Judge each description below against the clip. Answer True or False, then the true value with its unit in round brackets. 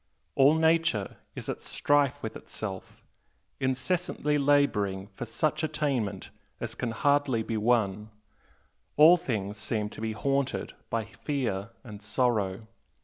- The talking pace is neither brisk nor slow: False (125 wpm)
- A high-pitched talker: False (120 Hz)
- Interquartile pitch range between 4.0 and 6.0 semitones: True (5.3 semitones)